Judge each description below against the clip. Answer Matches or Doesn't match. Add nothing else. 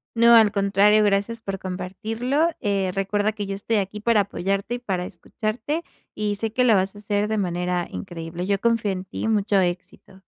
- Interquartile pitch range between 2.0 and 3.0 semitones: Matches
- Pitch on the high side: Matches